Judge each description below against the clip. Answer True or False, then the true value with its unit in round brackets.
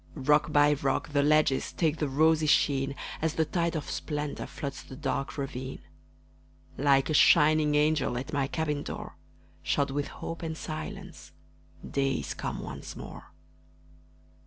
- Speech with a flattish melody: True (2.1 semitones)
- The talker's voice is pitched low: False (150 Hz)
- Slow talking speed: False (150 wpm)